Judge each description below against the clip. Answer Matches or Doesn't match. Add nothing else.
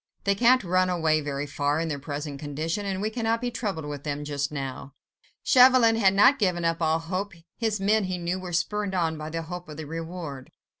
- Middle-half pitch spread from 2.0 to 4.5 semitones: Doesn't match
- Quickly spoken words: Matches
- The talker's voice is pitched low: Doesn't match